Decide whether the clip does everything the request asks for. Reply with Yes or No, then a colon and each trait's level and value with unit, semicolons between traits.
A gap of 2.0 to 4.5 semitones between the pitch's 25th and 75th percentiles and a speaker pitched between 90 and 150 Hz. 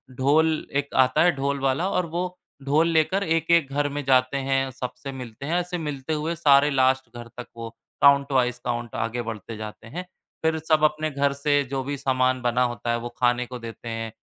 Yes: average, 3.8 semitones; low, 135 Hz